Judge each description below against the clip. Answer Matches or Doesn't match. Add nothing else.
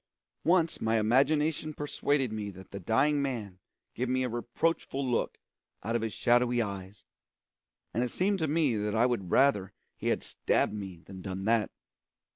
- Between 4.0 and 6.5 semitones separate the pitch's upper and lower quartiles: Matches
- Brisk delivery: Doesn't match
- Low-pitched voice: Matches